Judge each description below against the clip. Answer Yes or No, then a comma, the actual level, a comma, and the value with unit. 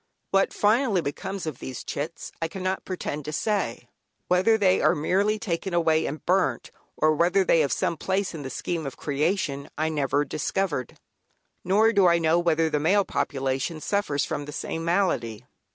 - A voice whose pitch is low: No, medium, 165 Hz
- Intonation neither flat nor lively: Yes, average, 4.6 semitones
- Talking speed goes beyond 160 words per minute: Yes, average, 175 wpm